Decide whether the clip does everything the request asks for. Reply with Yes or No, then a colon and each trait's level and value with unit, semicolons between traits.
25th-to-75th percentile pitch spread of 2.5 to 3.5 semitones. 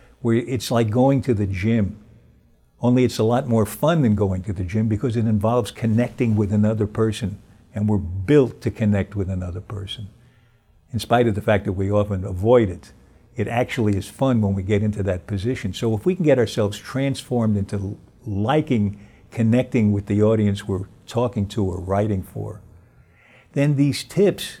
Yes: average, 3.2 semitones